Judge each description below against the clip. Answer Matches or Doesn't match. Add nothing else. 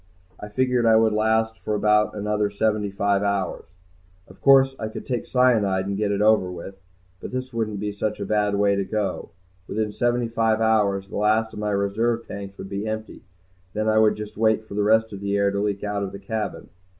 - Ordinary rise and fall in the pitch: Doesn't match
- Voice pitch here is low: Matches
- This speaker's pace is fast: Matches